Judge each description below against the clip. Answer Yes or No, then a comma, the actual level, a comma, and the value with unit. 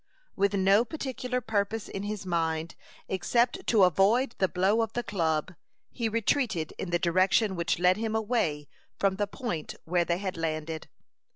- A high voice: Yes, high, 195 Hz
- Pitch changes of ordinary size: Yes, average, 4.5 semitones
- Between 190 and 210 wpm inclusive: No, average, 165 wpm